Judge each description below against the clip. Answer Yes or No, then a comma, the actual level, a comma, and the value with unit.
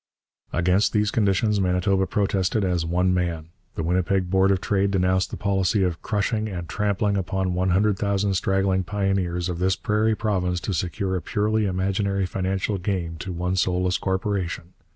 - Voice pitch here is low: Yes, very low, 95 Hz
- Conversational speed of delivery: Yes, average, 165 wpm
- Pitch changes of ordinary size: No, narrow, 1.8 semitones